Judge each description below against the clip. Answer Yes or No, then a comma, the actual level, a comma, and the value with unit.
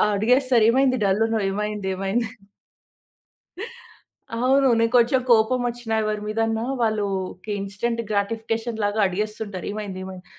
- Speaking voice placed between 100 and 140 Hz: No, high, 220 Hz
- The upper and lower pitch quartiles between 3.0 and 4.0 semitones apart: No, narrow, 2.4 semitones